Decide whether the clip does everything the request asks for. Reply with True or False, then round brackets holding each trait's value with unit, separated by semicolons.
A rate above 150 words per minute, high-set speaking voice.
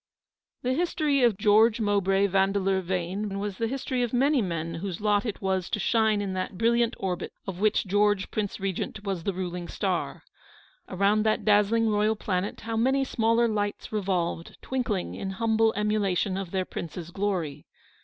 True (165 wpm; 205 Hz)